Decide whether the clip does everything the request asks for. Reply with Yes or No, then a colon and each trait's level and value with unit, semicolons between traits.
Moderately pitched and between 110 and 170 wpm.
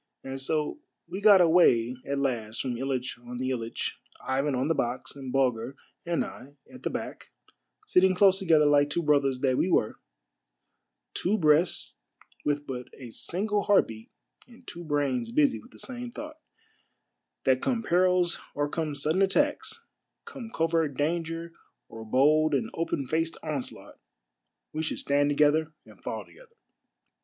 Yes: medium, 150 Hz; average, 160 wpm